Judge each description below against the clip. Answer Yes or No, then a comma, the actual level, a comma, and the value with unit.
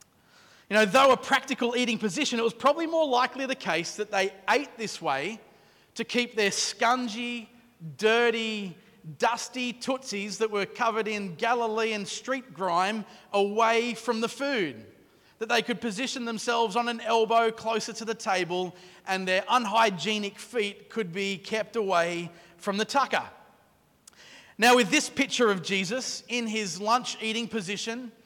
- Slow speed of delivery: No, average, 150 wpm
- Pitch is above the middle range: Yes, high, 225 Hz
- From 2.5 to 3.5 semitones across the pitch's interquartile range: Yes, average, 2.8 semitones